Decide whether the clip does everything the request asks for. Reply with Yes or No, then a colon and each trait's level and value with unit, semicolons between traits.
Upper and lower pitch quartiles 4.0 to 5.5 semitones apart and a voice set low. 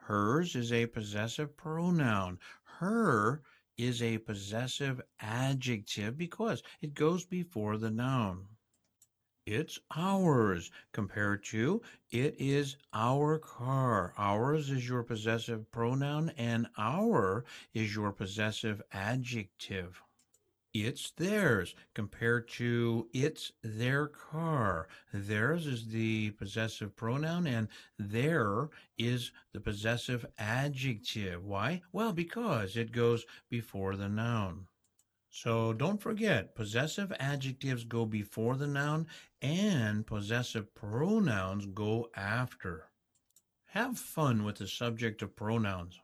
Yes: average, 5.1 semitones; low, 115 Hz